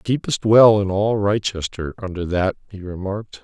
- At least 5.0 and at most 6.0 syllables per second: No, 4.8 syllables/s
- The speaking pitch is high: No, low, 100 Hz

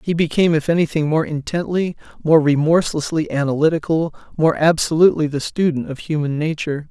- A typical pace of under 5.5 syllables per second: No, 6.0 syllables/s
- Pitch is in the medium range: Yes, medium, 155 Hz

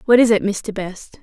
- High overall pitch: Yes, high, 210 Hz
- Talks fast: Yes, fast, 245 wpm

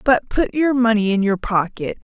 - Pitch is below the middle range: No, high, 225 Hz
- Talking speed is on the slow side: No, average, 200 wpm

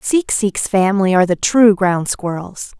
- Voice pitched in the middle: No, high, 200 Hz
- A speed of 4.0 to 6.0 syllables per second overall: Yes, 4.5 syllables/s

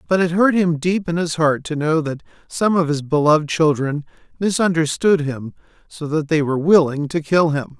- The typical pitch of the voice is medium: Yes, medium, 160 Hz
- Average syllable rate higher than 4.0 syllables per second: Yes, 5.2 syllables/s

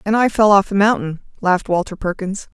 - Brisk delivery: Yes, fast, 210 wpm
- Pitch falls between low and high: No, high, 200 Hz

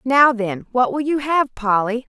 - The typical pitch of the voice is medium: No, high, 245 Hz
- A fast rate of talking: No, average, 195 wpm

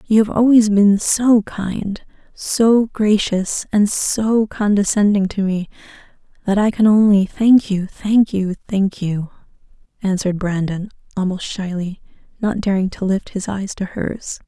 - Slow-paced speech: No, average, 145 wpm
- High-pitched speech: Yes, high, 200 Hz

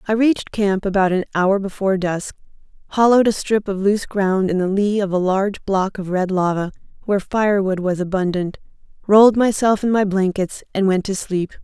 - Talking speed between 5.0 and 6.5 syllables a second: Yes, 5.5 syllables/s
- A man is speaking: No, female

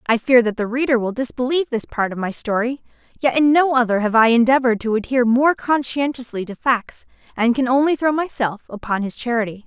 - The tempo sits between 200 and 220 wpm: Yes, fast, 205 wpm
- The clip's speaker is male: No, female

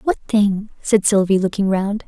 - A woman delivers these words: Yes, female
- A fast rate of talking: No, average, 175 wpm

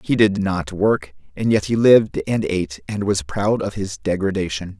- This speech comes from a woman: No, male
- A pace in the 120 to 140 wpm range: No, average, 200 wpm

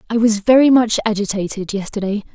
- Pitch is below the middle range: No, high, 215 Hz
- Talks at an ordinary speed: Yes, average, 155 wpm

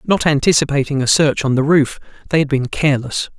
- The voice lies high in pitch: No, medium, 145 Hz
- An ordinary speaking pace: Yes, average, 195 wpm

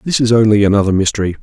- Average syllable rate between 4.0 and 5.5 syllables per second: No, 7.9 syllables/s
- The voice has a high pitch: No, low, 105 Hz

